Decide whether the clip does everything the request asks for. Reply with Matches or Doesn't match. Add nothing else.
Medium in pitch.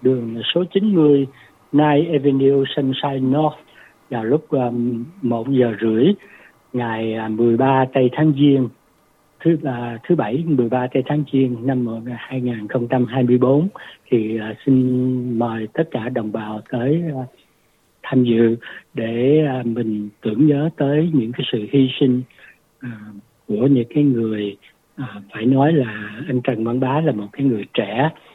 Doesn't match